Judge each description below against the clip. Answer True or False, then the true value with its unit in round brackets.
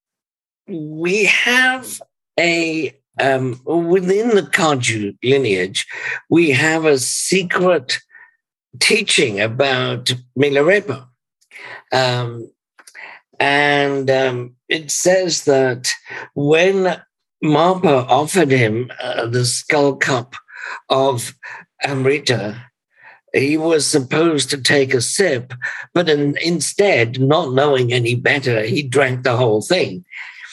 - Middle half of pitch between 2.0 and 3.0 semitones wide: False (4.9 semitones)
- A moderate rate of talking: False (100 wpm)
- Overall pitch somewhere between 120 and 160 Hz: True (140 Hz)